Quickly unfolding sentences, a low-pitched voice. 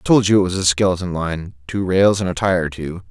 Yes: fast, 290 wpm; very low, 90 Hz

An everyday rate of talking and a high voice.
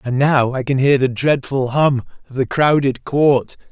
No: average, 180 wpm; low, 135 Hz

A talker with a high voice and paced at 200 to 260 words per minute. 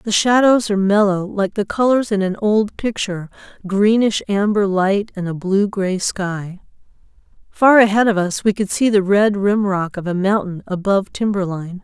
No: high, 200 Hz; average, 175 wpm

